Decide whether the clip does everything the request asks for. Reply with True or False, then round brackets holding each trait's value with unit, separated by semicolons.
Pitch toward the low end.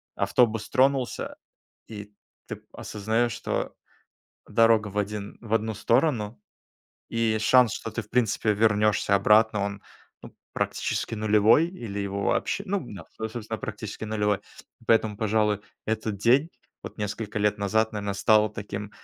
True (110 Hz)